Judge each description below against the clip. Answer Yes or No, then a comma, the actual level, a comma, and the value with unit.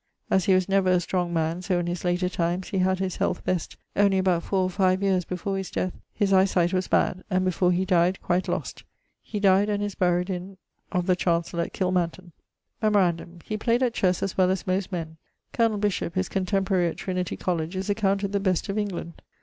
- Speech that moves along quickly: Yes, fast, 220 wpm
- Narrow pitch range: Yes, narrow, 1.6 semitones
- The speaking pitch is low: No, medium, 185 Hz